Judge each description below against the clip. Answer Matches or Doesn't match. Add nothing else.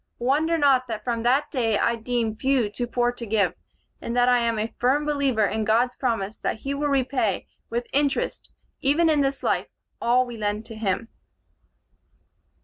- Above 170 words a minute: Matches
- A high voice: Matches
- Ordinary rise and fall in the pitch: Matches